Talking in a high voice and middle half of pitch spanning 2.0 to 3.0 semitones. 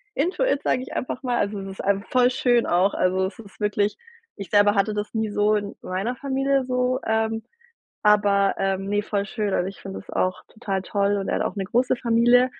No: high, 210 Hz; average, 3.6 semitones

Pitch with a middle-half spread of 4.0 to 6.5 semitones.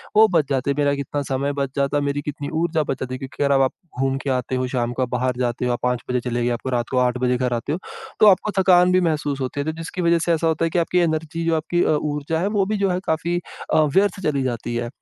Yes: average, 4.5 semitones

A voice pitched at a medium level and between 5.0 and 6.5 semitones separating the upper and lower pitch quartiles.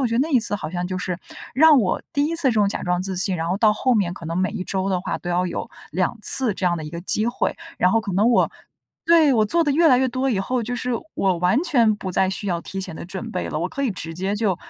No: high, 200 Hz; wide, 5.5 semitones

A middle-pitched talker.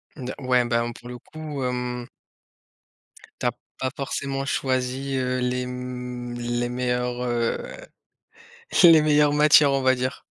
No: low, 125 Hz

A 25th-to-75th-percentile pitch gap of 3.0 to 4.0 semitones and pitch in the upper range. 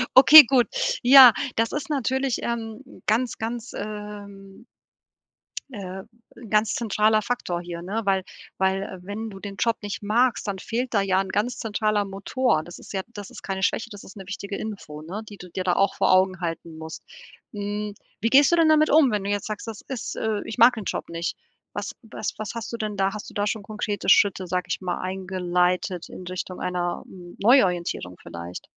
Yes: average, 3.3 semitones; high, 205 Hz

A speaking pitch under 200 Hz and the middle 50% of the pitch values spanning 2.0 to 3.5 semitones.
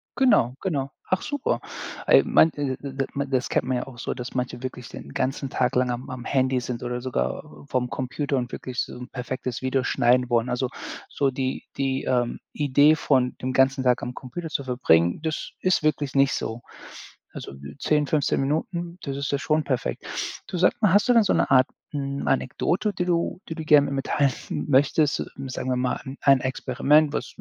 Yes: low, 135 Hz; average, 2.8 semitones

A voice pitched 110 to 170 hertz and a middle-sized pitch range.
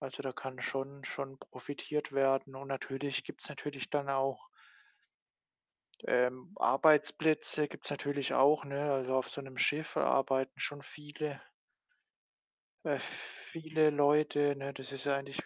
No: medium, 140 Hz; narrow, 1.6 semitones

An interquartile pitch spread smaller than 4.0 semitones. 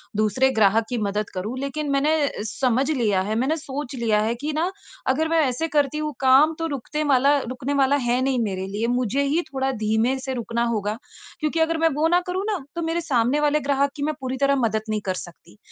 No: average, 4.8 semitones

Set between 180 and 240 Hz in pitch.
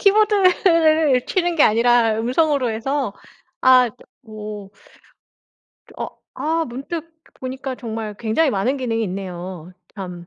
No: very high, 250 Hz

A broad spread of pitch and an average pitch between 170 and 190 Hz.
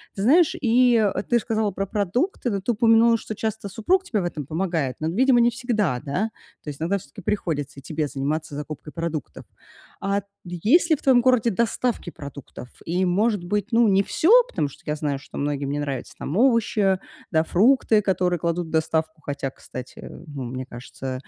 Yes: wide, 7.2 semitones; medium, 185 Hz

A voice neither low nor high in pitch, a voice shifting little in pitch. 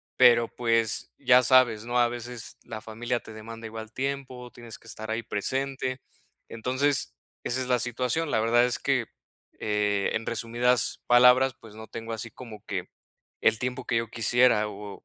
No: low, 120 Hz; narrow, 2.0 semitones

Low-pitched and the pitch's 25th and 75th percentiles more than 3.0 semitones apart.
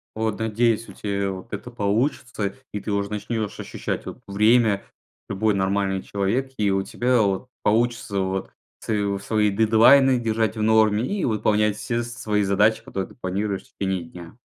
No: low, 105 Hz; narrow, 2.4 semitones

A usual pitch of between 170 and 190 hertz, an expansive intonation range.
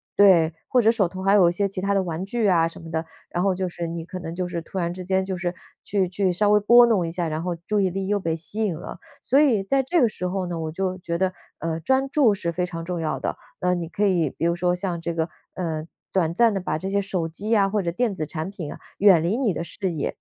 No: medium, 185 Hz; average, 3.0 semitones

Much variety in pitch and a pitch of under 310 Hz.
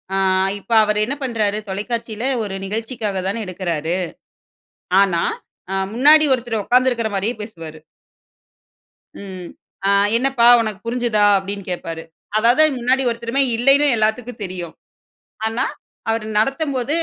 No: average, 4.1 semitones; high, 225 Hz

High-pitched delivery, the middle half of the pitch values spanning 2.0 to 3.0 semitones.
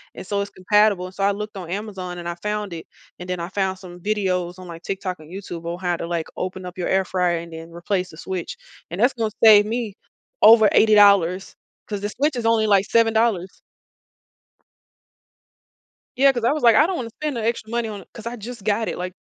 No: high, 200 Hz; average, 3.5 semitones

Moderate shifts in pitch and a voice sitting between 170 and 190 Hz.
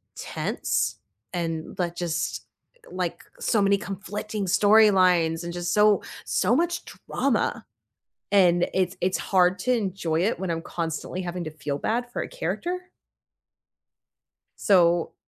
Yes: average, 3.3 semitones; medium, 185 Hz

